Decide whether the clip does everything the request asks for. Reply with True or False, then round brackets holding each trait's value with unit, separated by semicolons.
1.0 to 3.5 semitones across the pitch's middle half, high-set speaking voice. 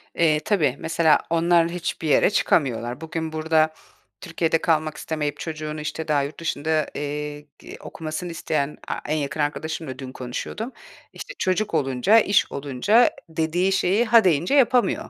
False (2.9 semitones; 160 Hz)